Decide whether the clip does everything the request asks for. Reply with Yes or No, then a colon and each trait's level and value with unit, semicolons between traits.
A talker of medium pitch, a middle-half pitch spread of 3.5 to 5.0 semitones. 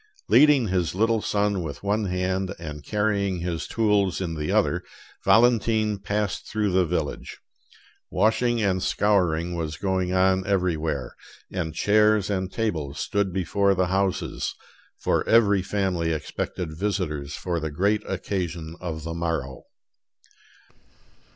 No: very low, 95 Hz; average, 3.8 semitones